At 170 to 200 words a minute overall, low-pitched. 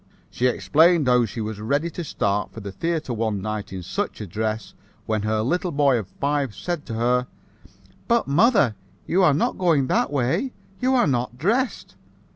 Yes: average, 185 wpm; low, 130 Hz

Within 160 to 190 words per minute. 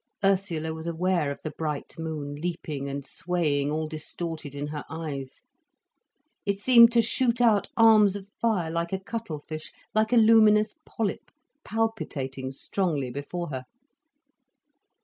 No: average, 140 wpm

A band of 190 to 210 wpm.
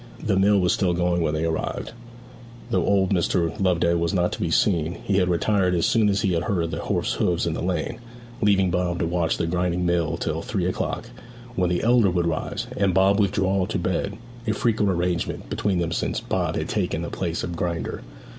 Yes: fast, 205 wpm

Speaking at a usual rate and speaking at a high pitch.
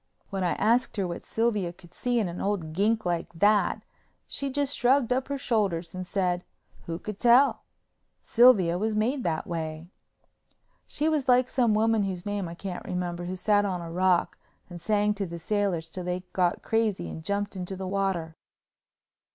Yes: average, 180 wpm; high, 195 Hz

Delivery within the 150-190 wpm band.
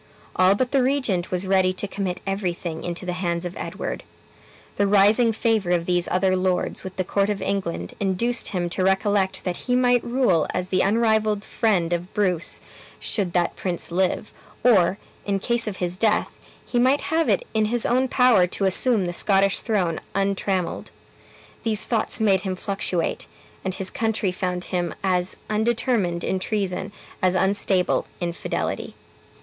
Yes: average, 165 wpm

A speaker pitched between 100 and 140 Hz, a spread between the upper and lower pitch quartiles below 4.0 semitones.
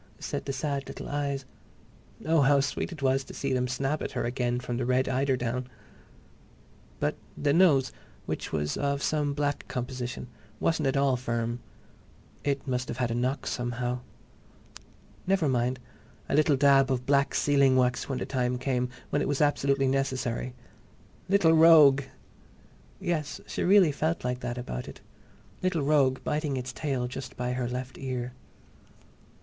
Yes: low, 135 Hz; narrow, 2.4 semitones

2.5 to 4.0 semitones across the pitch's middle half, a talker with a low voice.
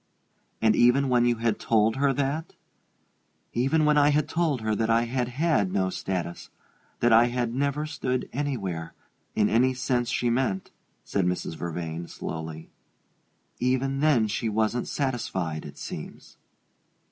No: average, 4.9 semitones; low, 120 Hz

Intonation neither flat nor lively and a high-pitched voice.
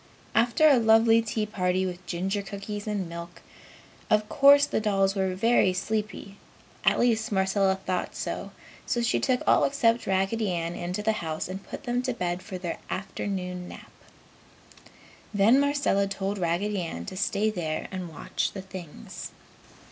Yes: average, 3.3 semitones; high, 195 Hz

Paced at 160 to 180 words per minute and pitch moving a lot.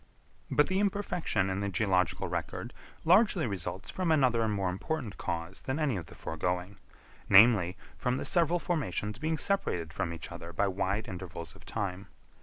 Yes: average, 170 wpm; wide, 9.0 semitones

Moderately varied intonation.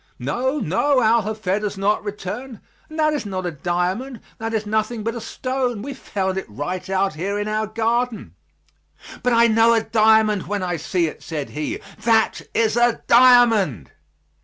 Yes: average, 3.8 semitones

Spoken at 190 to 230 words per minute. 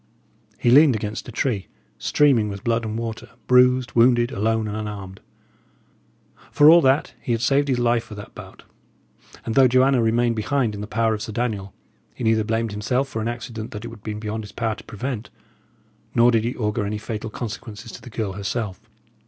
Yes: average, 200 wpm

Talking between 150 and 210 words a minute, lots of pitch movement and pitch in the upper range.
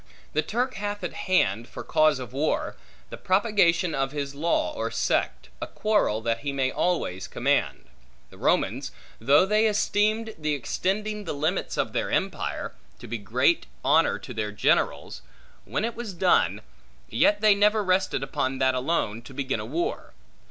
No: average, 165 wpm; wide, 7.9 semitones; medium, 165 Hz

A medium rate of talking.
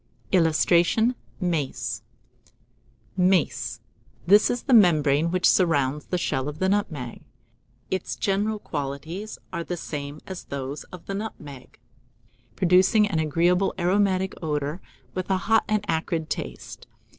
No: slow, 125 wpm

